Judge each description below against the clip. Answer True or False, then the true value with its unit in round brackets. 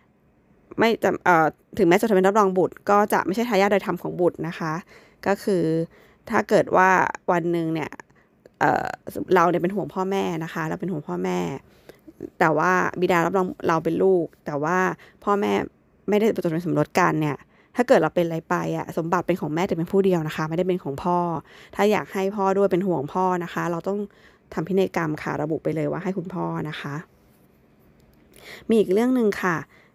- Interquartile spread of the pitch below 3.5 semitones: True (2.8 semitones)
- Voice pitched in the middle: True (180 Hz)